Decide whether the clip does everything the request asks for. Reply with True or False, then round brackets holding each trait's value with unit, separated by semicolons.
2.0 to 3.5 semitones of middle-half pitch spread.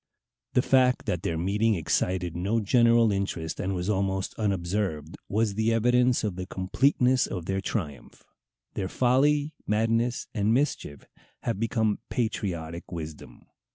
False (4.3 semitones)